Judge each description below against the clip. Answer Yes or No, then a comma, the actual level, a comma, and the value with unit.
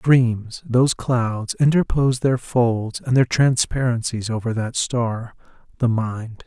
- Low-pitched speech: Yes, low, 120 Hz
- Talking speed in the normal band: No, slow, 130 wpm